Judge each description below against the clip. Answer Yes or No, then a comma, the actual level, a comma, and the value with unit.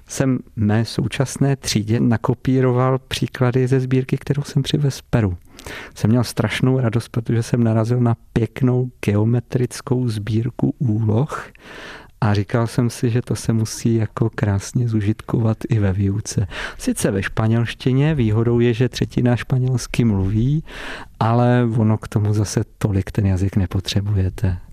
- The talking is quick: No, average, 135 wpm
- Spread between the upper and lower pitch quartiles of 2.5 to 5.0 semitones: Yes, average, 2.9 semitones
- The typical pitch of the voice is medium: No, low, 115 Hz